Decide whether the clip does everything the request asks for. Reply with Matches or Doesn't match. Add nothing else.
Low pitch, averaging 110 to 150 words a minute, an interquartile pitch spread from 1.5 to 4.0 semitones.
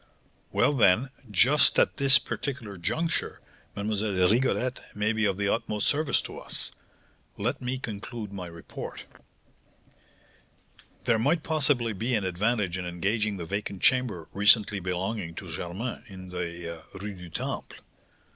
Doesn't match